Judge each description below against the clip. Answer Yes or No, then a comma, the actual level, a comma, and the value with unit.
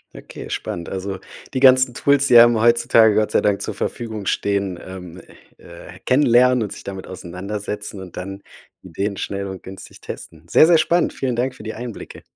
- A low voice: Yes, low, 105 Hz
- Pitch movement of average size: Yes, average, 4.2 semitones